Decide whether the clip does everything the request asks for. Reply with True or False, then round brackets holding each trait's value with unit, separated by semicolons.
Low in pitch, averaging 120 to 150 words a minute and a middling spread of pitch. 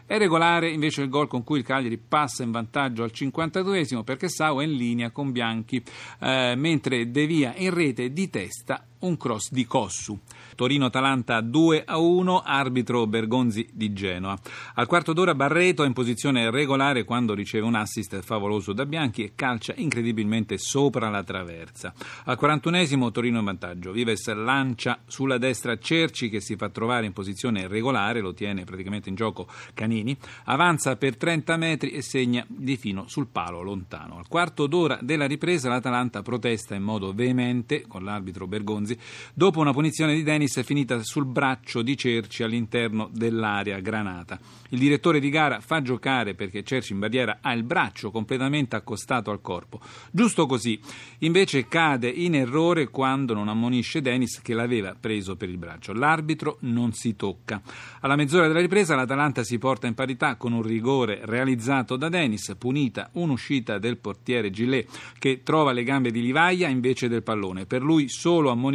False (125 Hz; 170 wpm; 4.2 semitones)